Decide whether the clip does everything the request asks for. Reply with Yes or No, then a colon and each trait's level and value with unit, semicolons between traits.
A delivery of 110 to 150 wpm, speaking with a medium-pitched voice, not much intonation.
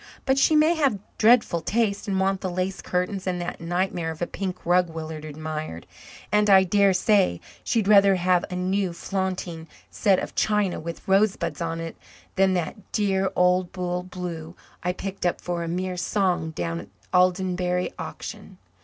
No: average, 175 wpm; medium, 180 Hz; narrow, 2.1 semitones